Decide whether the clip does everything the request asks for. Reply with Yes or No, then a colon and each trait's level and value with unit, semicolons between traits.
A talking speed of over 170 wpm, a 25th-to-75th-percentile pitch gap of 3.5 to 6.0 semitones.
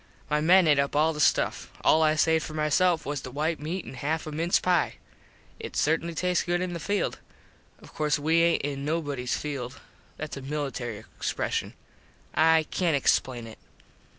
No: average, 185 wpm; average, 2.7 semitones